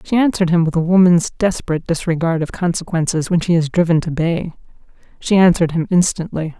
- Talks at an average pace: Yes, average, 175 wpm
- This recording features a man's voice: No, female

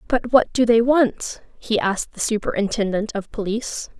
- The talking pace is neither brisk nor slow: Yes, average, 165 wpm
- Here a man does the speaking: No, female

